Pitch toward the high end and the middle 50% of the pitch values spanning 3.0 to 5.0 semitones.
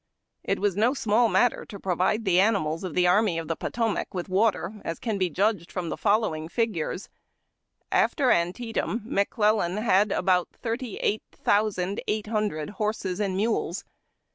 Yes: high, 205 Hz; average, 3.4 semitones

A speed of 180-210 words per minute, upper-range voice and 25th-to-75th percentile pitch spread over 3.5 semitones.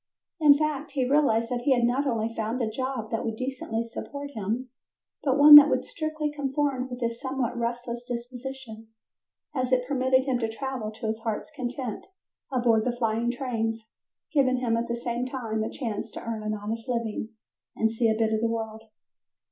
No: average, 190 wpm; high, 240 Hz; average, 2.8 semitones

